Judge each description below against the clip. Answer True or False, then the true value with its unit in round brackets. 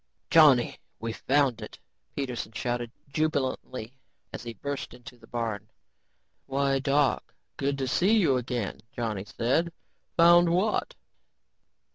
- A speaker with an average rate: False (120 wpm)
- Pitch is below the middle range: True (130 Hz)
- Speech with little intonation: False (3.4 semitones)